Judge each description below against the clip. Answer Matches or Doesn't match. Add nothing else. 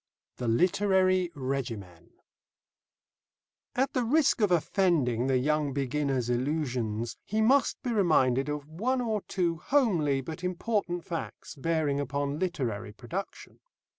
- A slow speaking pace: Matches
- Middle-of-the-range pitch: Matches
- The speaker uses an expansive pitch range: Matches